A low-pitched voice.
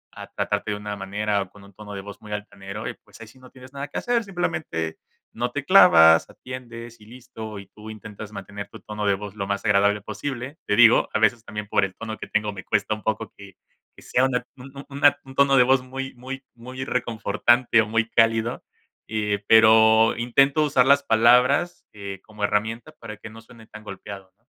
Yes: low, 110 Hz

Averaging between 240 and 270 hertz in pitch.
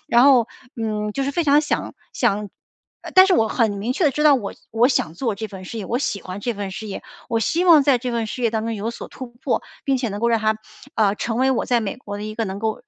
No: high, 230 Hz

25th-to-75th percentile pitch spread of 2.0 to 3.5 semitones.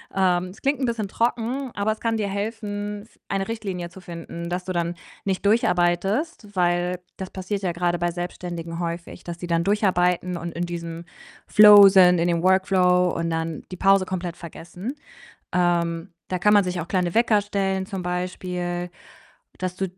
Yes: narrow, 2.5 semitones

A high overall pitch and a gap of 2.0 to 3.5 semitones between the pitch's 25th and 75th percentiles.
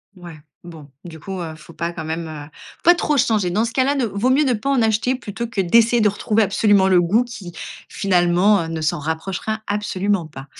No: high, 195 Hz; average, 4.9 semitones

